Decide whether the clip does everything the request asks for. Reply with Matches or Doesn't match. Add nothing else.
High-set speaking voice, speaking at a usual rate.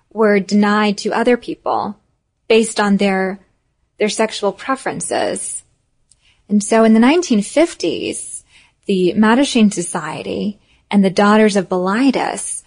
Doesn't match